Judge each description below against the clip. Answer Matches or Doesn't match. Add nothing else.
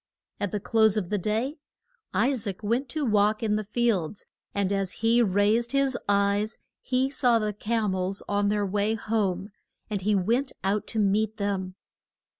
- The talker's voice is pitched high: Matches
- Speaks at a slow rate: Doesn't match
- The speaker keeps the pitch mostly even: Matches